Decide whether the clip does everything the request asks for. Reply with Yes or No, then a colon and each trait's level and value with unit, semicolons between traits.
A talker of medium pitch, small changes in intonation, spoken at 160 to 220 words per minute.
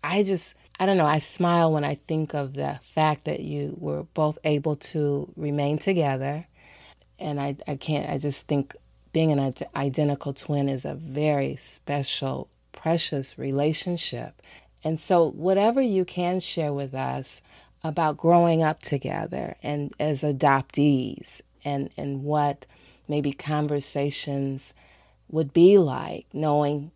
No: medium, 150 Hz; narrow, 2.3 semitones; average, 140 wpm